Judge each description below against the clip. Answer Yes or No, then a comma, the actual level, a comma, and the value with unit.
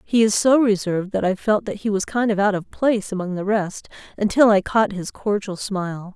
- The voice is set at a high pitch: Yes, high, 205 Hz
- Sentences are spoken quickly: Yes, fast, 235 wpm